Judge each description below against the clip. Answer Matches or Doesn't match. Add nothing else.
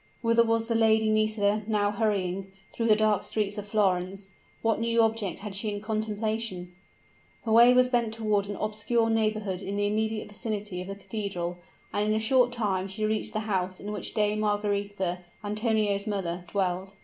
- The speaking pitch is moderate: Doesn't match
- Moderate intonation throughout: Doesn't match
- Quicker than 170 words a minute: Matches